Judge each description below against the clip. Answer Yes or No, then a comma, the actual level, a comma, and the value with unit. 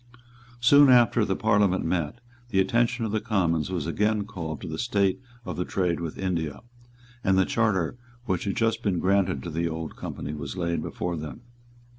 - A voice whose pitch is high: No, very low, 95 Hz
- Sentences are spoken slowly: No, average, 185 wpm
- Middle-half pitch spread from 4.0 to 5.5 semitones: Yes, average, 4.5 semitones